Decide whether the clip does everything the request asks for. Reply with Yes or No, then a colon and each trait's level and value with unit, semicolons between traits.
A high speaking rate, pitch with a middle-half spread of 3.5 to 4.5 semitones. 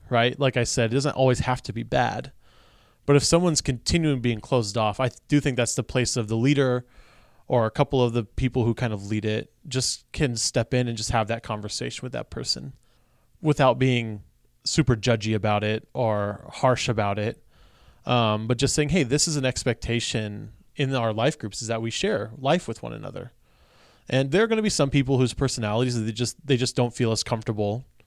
No: fast, 210 wpm; average, 3.1 semitones